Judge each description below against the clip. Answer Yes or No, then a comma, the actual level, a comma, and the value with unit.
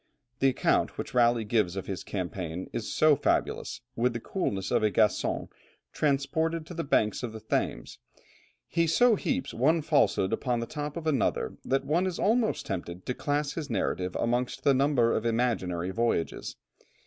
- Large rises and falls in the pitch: Yes, wide, 6.2 semitones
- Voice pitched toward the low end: Yes, low, 125 Hz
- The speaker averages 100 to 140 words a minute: No, average, 170 wpm